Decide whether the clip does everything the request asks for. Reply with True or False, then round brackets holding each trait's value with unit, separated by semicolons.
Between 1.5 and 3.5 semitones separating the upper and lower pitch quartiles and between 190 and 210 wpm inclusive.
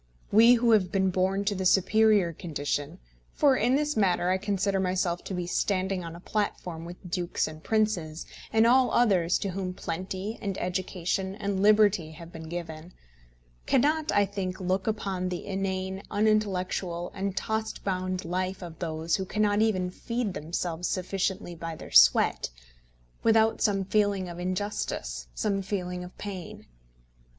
False (2.6 semitones; 155 wpm)